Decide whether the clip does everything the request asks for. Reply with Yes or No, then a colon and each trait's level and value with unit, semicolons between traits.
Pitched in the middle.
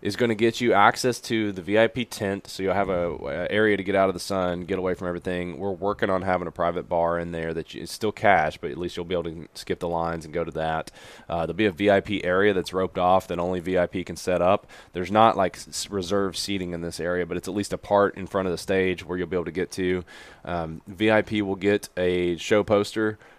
No: very low, 95 Hz